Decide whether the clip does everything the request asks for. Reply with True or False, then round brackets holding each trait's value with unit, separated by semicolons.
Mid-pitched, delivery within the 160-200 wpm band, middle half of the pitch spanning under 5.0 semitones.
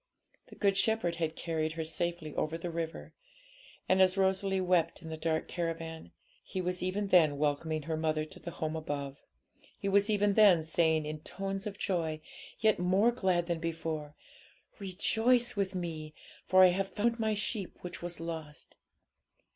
True (175 Hz; 170 wpm; 3.4 semitones)